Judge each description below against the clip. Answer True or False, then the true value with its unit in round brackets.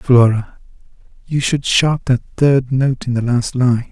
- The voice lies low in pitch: True (125 Hz)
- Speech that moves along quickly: False (170 wpm)